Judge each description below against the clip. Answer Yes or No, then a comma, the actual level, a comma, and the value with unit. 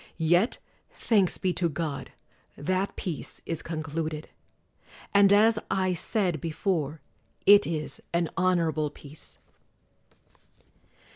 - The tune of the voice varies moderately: Yes, average, 3.4 semitones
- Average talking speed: No, slow, 100 wpm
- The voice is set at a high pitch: No, medium, 170 Hz